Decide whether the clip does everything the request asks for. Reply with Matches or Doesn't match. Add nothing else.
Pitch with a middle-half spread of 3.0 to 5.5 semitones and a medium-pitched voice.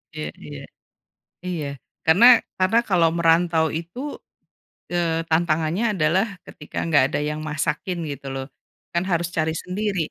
Doesn't match